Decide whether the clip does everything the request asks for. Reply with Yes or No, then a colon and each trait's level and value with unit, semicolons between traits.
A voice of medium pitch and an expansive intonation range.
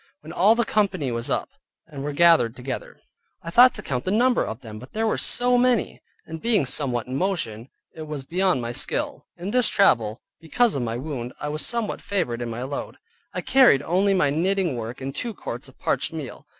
Yes: medium, 155 Hz; wide, 7.9 semitones